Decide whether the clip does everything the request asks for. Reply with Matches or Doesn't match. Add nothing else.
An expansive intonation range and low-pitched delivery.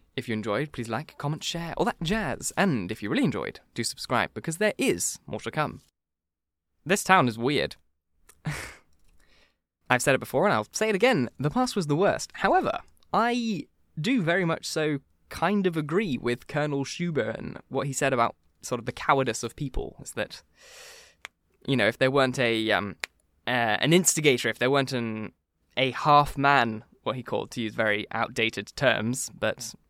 Matches